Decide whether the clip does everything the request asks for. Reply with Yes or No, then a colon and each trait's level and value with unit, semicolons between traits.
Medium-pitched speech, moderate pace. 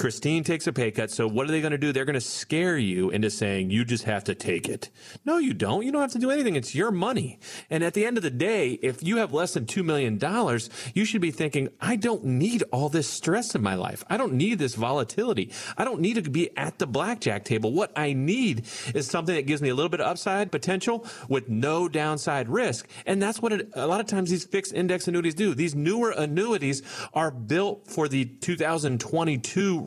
No: medium, 160 Hz; fast, 235 wpm